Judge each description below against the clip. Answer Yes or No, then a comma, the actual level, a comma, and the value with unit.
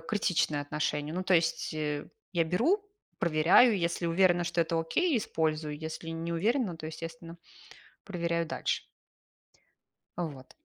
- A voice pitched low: No, medium, 165 Hz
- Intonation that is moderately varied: No, narrow, 2.3 semitones